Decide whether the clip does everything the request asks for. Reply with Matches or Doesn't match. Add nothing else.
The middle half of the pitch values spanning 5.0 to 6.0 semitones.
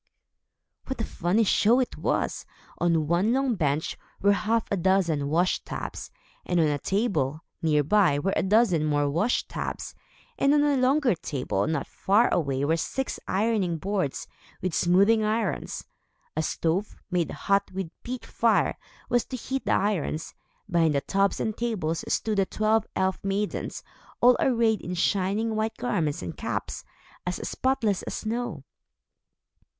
Matches